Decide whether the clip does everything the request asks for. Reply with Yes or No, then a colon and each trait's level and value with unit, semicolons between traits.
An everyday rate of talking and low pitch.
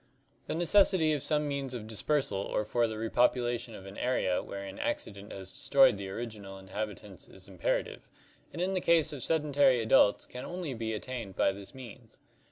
Yes: average, 180 wpm; low, 120 Hz